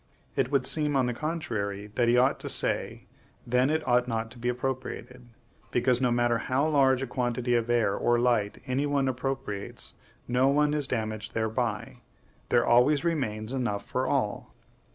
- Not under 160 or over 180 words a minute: Yes, average, 175 wpm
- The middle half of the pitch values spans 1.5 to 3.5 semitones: Yes, narrow, 2.4 semitones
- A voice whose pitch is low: Yes, low, 125 Hz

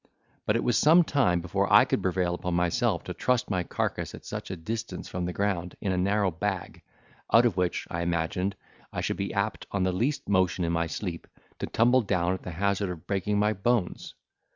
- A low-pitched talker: Yes, very low, 95 Hz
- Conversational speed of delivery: No, fast, 215 wpm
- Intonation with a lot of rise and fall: No, average, 3.0 semitones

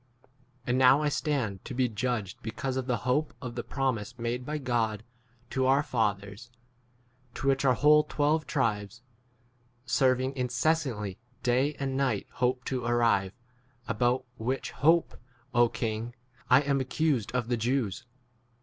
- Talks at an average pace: Yes, average, 150 wpm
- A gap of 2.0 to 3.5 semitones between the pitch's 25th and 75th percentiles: Yes, average, 2.7 semitones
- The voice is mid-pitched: No, low, 125 Hz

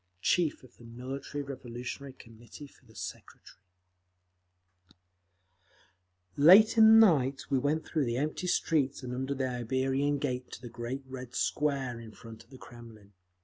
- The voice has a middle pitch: No, low, 130 Hz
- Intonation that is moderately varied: Yes, average, 3.0 semitones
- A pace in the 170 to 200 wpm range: No, average, 150 wpm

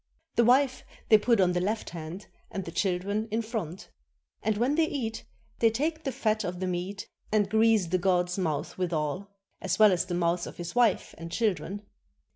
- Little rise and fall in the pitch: No, average, 4.0 semitones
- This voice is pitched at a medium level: No, high, 200 Hz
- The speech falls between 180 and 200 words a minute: Yes, average, 195 wpm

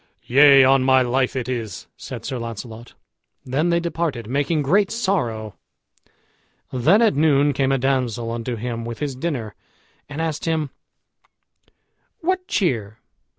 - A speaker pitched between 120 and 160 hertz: Yes, low, 135 Hz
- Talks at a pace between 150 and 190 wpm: No, average, 140 wpm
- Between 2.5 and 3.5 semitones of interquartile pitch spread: No, average, 5.1 semitones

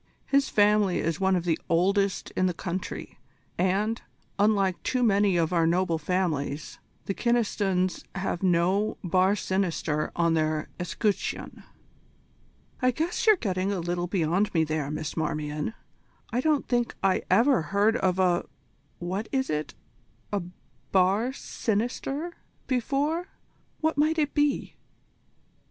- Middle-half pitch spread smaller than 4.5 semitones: No, average, 4.8 semitones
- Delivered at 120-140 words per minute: Yes, slow, 135 wpm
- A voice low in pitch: No, high, 190 Hz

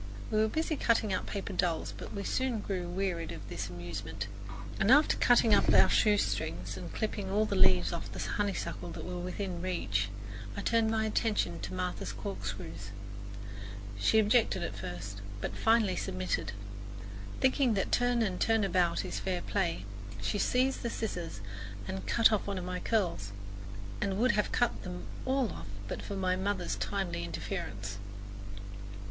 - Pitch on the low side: No, high, 190 Hz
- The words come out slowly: No, average, 165 wpm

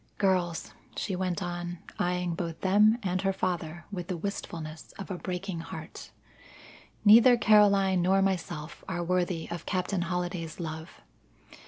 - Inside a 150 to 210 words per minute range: No, average, 140 wpm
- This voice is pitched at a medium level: Yes, medium, 180 Hz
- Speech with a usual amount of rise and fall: No, narrow, 2.1 semitones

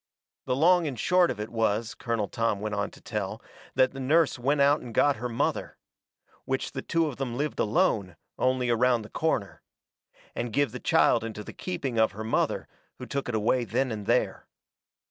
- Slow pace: No, average, 200 wpm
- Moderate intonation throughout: Yes, average, 4.0 semitones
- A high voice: No, low, 120 Hz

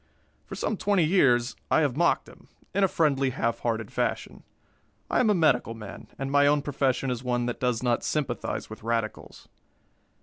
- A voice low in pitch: Yes, low, 130 Hz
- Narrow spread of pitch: No, average, 4.1 semitones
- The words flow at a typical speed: Yes, average, 180 wpm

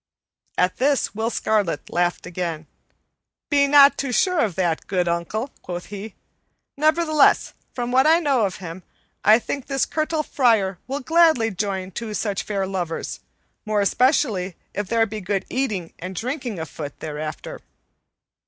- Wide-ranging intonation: Yes, wide, 6.8 semitones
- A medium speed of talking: Yes, average, 150 wpm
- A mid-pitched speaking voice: No, high, 215 Hz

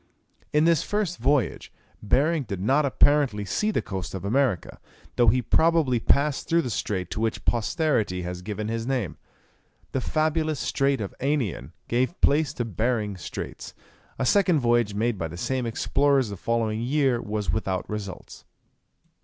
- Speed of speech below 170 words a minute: Yes, average, 160 wpm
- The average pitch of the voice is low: Yes, low, 120 Hz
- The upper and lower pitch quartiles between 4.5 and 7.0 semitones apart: Yes, wide, 5.6 semitones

